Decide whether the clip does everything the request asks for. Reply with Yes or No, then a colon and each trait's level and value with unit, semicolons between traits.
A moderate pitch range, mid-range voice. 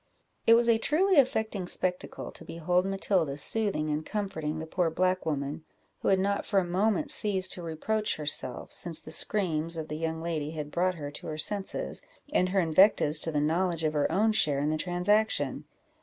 Yes: average, 4.3 semitones; medium, 175 Hz